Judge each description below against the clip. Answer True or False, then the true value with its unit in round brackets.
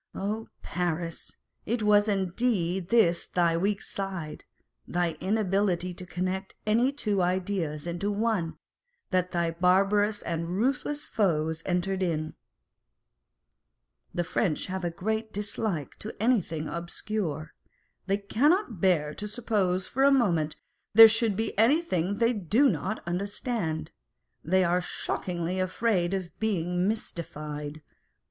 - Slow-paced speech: True (125 wpm)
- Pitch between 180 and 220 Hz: True (190 Hz)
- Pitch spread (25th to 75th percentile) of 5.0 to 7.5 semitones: False (4.0 semitones)